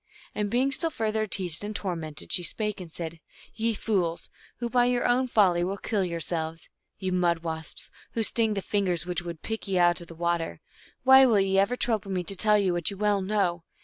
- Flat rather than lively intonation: No, average, 3.9 semitones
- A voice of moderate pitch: No, high, 195 Hz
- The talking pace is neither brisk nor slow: No, fast, 215 wpm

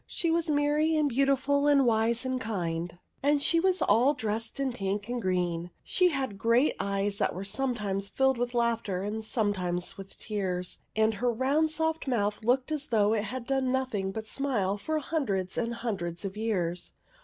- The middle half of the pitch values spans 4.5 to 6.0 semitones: Yes, wide, 5.5 semitones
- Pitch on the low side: No, high, 230 Hz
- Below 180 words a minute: No, average, 195 wpm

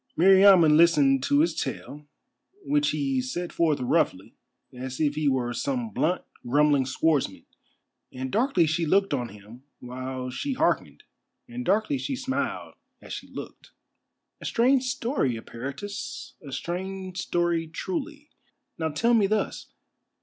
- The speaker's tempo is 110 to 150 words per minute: Yes, slow, 135 wpm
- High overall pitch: No, medium, 165 Hz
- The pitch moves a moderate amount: No, wide, 8.3 semitones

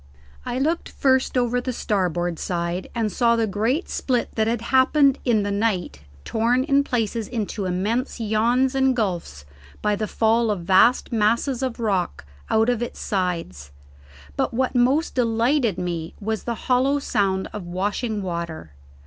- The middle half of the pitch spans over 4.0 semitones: Yes, average, 4.6 semitones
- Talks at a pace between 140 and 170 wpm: Yes, average, 155 wpm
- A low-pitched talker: No, high, 225 Hz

